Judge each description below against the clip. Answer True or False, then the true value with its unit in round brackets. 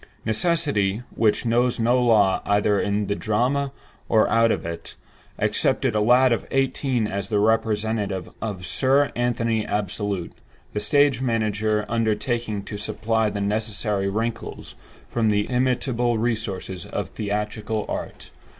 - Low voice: True (110 Hz)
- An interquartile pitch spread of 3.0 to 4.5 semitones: False (2.6 semitones)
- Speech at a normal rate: False (130 wpm)